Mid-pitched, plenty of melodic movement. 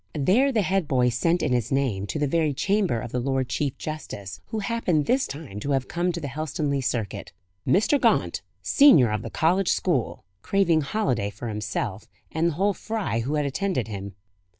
Yes: medium, 145 Hz; wide, 6.9 semitones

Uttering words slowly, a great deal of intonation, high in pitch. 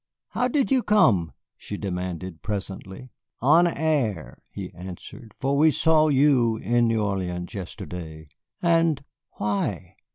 No: slow, 125 wpm; wide, 8.4 semitones; low, 110 Hz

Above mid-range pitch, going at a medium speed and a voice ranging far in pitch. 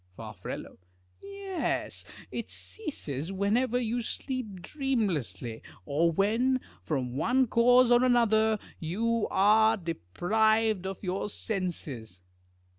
No: high, 215 Hz; slow, 100 wpm; wide, 6.5 semitones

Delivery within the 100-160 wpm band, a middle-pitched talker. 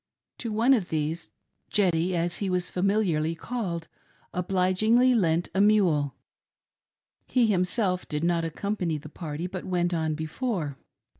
Yes: slow, 135 wpm; medium, 180 Hz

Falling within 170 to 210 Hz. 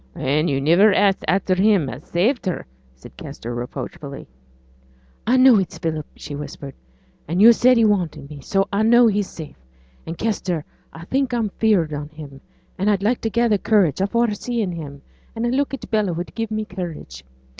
Yes: high, 190 Hz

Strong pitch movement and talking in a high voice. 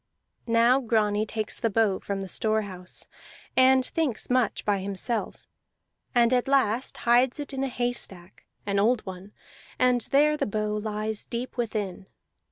No: average, 3.4 semitones; high, 225 Hz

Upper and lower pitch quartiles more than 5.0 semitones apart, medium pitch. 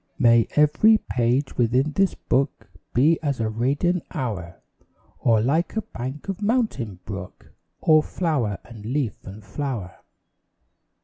No: wide, 5.6 semitones; low, 130 Hz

